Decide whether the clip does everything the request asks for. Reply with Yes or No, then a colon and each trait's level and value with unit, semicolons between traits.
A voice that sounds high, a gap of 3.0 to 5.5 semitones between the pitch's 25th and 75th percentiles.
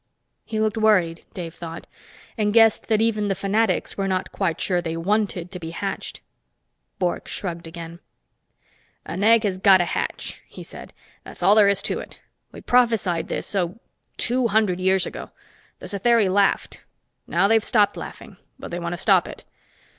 Yes: high, 195 Hz; average, 3.6 semitones